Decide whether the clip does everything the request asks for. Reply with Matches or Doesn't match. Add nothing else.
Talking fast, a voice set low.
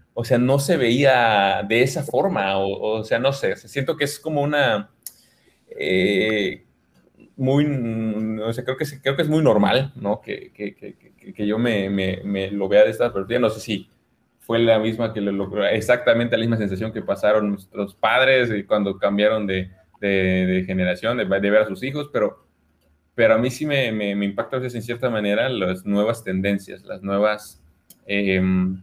Matches